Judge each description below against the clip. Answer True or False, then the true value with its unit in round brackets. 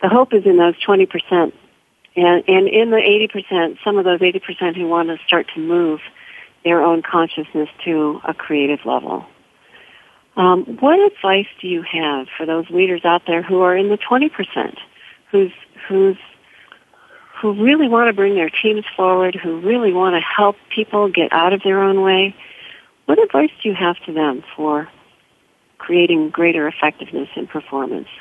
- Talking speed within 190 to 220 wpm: False (170 wpm)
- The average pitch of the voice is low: False (185 Hz)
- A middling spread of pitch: True (3.6 semitones)